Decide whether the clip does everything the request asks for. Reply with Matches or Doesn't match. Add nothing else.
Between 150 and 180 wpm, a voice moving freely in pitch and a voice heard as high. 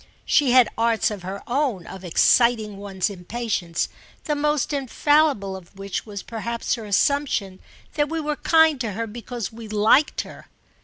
Matches